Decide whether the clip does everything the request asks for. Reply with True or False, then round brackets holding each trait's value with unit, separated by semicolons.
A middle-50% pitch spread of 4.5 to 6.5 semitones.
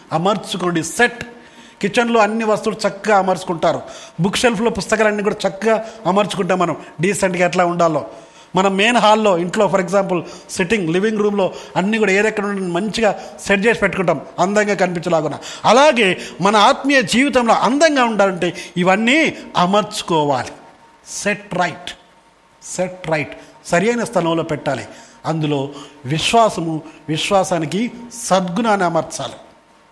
False (3.5 semitones)